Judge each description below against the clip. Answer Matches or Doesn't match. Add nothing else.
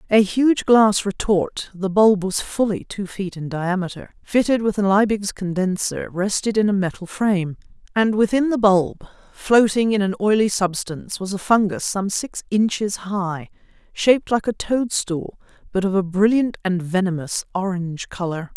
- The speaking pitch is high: Matches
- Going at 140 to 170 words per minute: Matches